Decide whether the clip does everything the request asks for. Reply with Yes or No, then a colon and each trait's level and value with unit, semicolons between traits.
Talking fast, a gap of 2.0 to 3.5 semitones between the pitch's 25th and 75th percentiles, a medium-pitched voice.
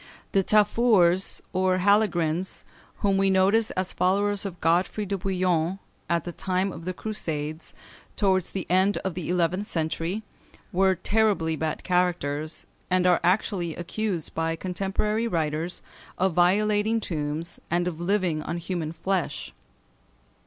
No: slow, 135 wpm; average, 2.8 semitones; medium, 180 Hz